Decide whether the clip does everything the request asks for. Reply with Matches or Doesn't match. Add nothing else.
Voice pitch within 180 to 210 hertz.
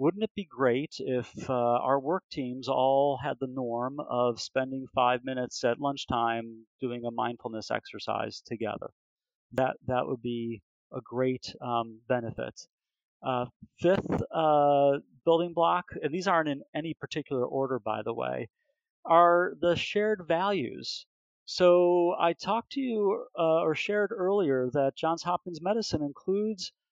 Doesn't match